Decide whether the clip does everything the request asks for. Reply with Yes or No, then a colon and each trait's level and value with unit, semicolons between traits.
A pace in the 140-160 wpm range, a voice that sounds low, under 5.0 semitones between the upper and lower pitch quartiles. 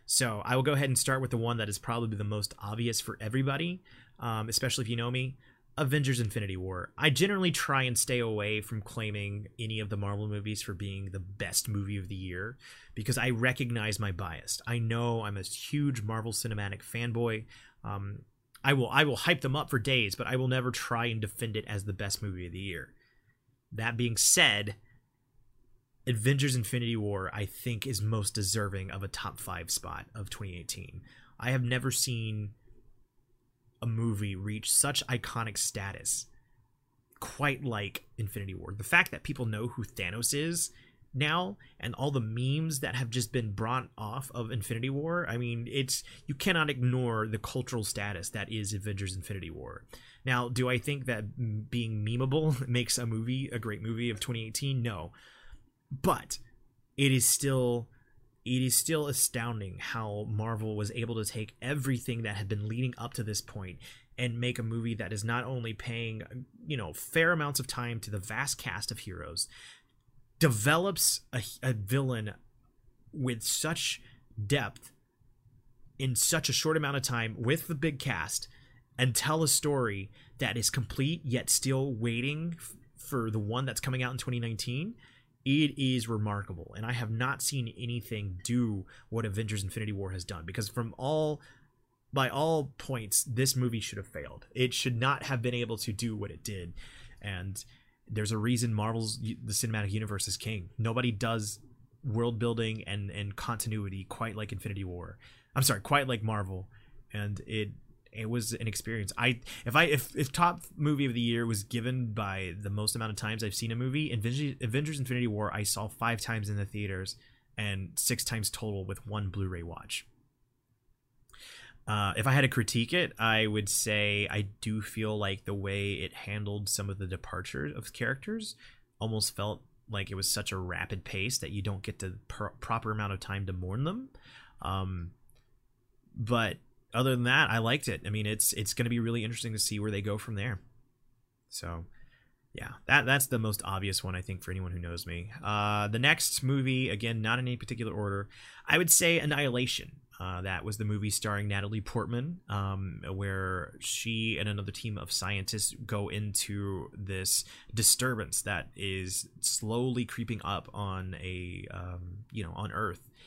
No: average, 180 wpm; low, 115 Hz; average, 3.4 semitones